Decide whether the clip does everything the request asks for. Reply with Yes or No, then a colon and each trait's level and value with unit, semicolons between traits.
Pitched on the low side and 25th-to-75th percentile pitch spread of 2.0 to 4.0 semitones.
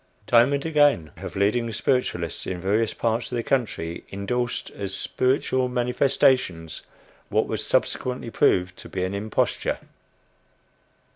No: low, 115 Hz; average, 4.8 semitones